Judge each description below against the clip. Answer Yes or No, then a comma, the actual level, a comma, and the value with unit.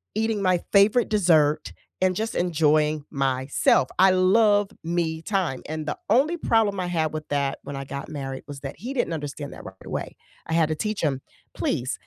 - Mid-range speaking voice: Yes, medium, 160 Hz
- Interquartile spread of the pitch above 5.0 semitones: Yes, wide, 5.4 semitones